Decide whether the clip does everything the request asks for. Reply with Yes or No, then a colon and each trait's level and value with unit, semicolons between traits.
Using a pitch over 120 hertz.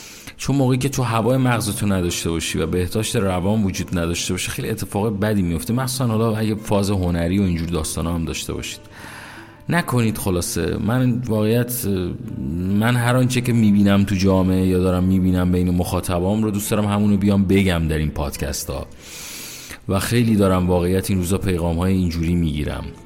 No: very low, 95 Hz